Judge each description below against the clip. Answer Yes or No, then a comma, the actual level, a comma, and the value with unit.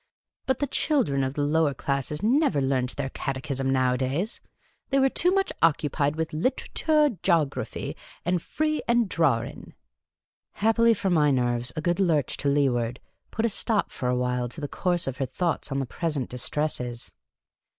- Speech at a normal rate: Yes, average, 170 wpm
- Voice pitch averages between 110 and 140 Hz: No, medium, 150 Hz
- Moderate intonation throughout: No, wide, 6.8 semitones